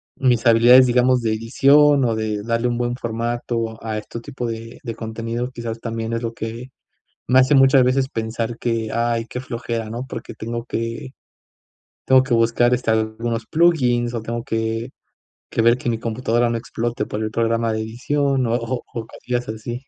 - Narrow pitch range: Yes, narrow, 1.6 semitones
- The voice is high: No, low, 115 Hz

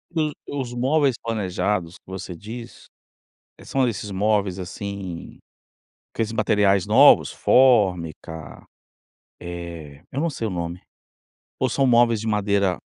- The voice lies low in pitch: Yes, low, 105 Hz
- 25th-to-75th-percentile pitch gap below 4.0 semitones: No, average, 4.8 semitones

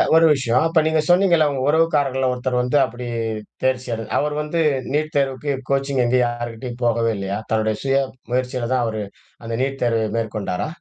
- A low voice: Yes, low, 130 Hz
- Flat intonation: No, average, 3.4 semitones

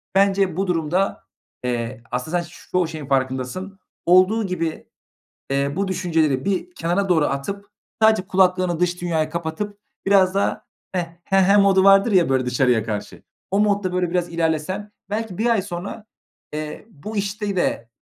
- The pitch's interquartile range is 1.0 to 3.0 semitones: No, average, 4.0 semitones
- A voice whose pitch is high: No, medium, 180 Hz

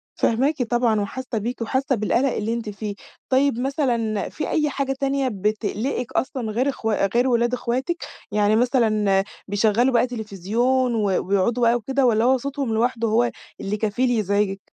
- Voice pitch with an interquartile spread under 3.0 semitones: No, average, 3.4 semitones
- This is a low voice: No, high, 235 Hz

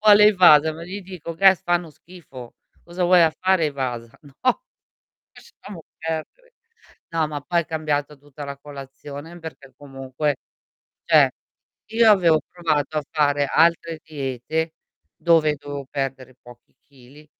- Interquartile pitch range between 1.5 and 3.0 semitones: No, average, 3.5 semitones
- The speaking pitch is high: No, medium, 155 Hz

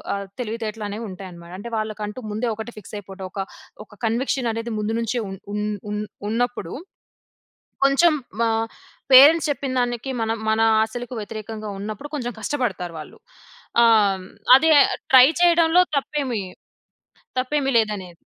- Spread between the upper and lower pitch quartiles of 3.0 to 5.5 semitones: Yes, average, 3.6 semitones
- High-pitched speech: Yes, high, 225 Hz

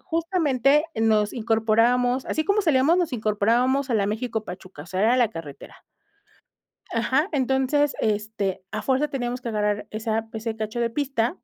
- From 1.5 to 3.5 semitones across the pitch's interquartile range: No, average, 3.9 semitones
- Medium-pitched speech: No, high, 235 Hz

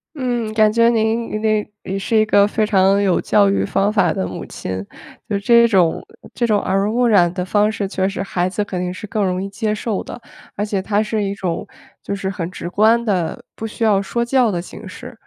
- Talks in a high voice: Yes, high, 205 Hz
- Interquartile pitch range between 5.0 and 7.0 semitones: No, narrow, 2.4 semitones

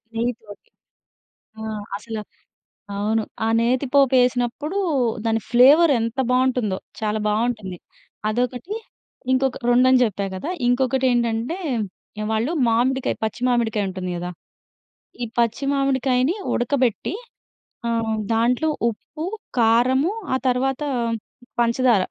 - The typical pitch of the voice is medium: No, high, 245 Hz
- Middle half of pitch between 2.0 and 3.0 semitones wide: Yes, average, 2.7 semitones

